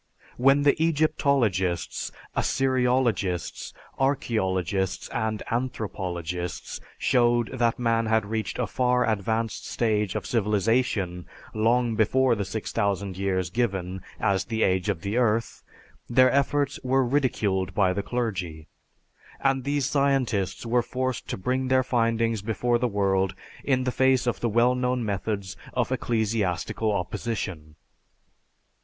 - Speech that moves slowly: Yes, slow, 125 wpm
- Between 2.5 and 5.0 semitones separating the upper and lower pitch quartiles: Yes, average, 4.5 semitones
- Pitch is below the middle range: Yes, low, 115 Hz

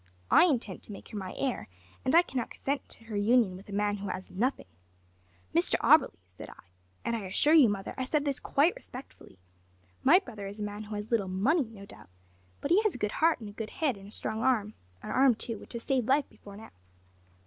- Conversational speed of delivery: No, fast, 235 wpm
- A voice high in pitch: Yes, high, 225 Hz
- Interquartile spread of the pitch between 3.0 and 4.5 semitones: No, average, 5.0 semitones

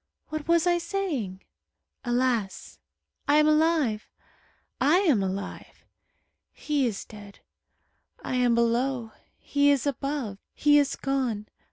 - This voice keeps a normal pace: No, slow, 120 wpm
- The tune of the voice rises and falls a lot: No, average, 5.0 semitones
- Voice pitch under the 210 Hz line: No, very high, 270 Hz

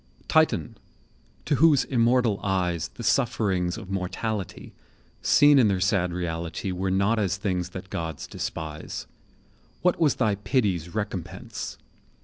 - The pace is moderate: No, slow, 130 wpm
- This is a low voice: Yes, very low, 95 Hz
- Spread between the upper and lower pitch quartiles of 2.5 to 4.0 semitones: No, average, 4.4 semitones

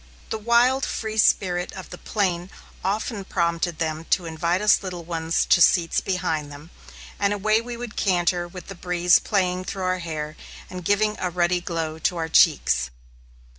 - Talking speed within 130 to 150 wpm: No, average, 170 wpm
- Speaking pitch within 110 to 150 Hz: No, medium, 180 Hz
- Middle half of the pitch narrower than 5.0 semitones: Yes, average, 3.0 semitones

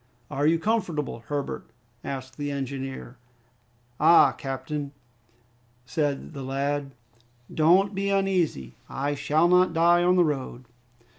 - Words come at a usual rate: No, slow, 120 wpm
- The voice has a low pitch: No, medium, 145 Hz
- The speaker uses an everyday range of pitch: Yes, average, 4.0 semitones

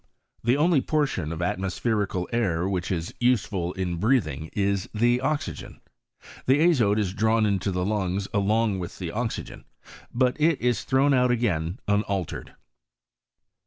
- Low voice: Yes, low, 105 Hz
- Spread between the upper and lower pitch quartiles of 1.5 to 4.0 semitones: No, average, 5.0 semitones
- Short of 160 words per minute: Yes, average, 140 wpm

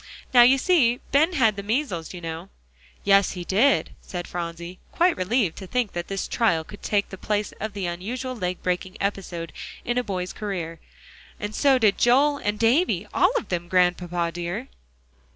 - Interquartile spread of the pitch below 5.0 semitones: No, wide, 5.5 semitones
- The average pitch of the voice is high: Yes, high, 200 Hz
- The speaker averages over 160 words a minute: Yes, average, 180 wpm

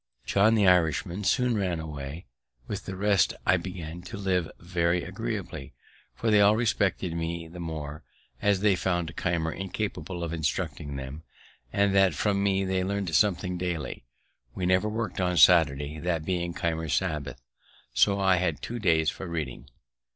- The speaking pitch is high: No, very low, 90 Hz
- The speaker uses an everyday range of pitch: Yes, average, 3.2 semitones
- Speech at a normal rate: Yes, average, 160 wpm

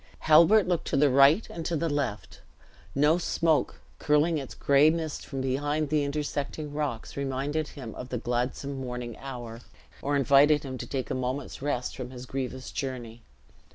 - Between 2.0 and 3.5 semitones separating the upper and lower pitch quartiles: Yes, average, 2.7 semitones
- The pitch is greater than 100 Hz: Yes, medium, 140 Hz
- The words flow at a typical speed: Yes, average, 170 wpm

